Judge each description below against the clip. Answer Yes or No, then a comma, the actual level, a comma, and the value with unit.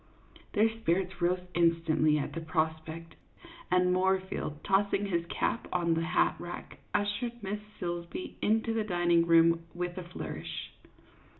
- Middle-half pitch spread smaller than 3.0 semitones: Yes, narrow, 2.6 semitones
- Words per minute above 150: No, average, 145 wpm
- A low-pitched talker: No, medium, 175 Hz